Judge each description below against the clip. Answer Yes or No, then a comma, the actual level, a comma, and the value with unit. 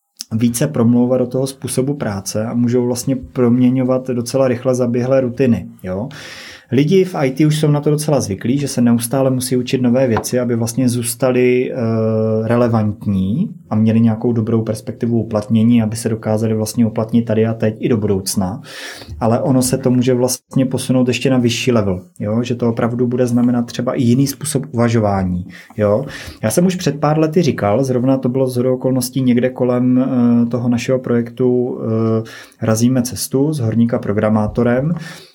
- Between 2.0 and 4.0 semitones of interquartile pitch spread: Yes, narrow, 2.5 semitones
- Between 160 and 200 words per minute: Yes, average, 165 wpm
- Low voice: Yes, low, 125 Hz